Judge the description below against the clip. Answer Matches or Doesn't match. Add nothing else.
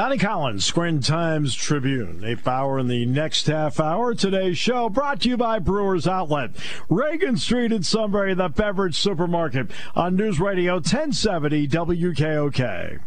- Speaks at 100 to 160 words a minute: Matches